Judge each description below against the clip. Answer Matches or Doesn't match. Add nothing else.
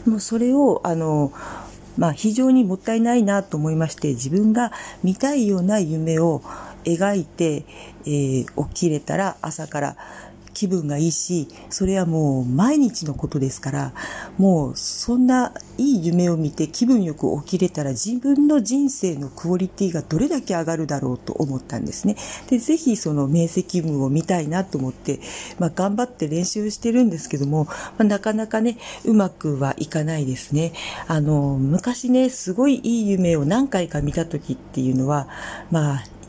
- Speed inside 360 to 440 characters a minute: Doesn't match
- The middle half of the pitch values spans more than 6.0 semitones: Matches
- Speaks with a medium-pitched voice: Matches